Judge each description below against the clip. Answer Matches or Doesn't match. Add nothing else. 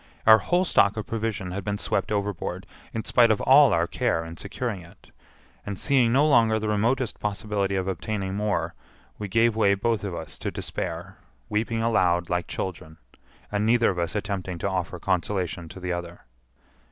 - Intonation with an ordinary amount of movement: Matches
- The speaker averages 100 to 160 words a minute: Doesn't match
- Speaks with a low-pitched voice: Matches